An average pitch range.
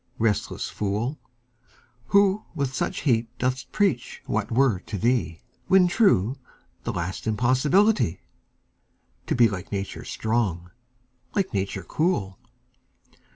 No: wide, 6.8 semitones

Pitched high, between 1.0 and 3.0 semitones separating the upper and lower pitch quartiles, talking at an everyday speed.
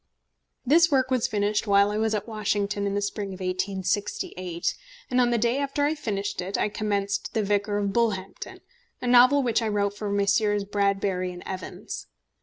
Yes: high, 205 Hz; narrow, 2.5 semitones; average, 185 wpm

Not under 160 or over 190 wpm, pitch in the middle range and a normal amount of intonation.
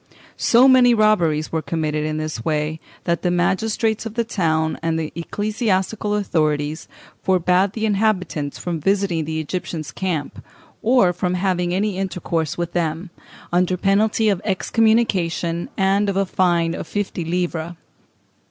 No: average, 145 wpm; medium, 180 Hz; average, 4.1 semitones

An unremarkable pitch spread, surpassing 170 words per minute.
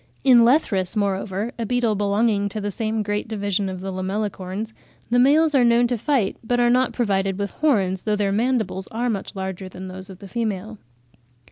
Yes: average, 3.6 semitones; average, 195 wpm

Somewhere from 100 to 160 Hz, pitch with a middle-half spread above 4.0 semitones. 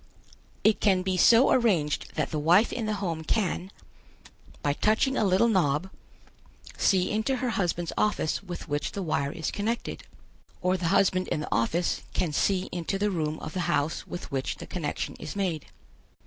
No: medium, 180 Hz; average, 4.5 semitones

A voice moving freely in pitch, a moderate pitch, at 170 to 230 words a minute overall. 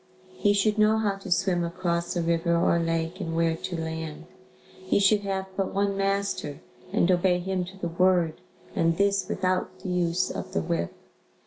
No: average, 2.8 semitones; medium, 180 Hz; average, 185 wpm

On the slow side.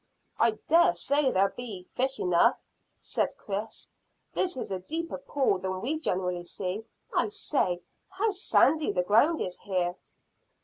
No: average, 145 wpm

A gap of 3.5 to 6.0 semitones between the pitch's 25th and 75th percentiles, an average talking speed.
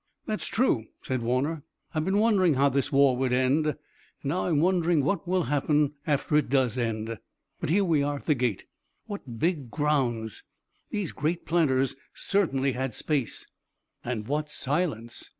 Yes: average, 4.5 semitones; average, 165 wpm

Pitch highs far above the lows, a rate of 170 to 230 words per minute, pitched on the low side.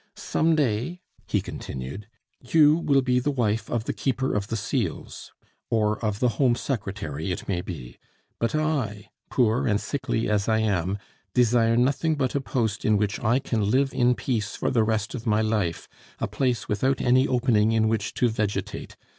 No: average, 3.6 semitones; average, 180 wpm; low, 115 Hz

